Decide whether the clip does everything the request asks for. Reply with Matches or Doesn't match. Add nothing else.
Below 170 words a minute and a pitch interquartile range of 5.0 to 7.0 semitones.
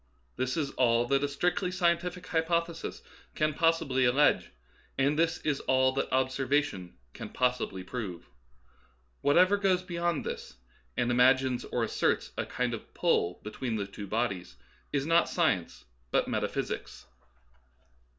Matches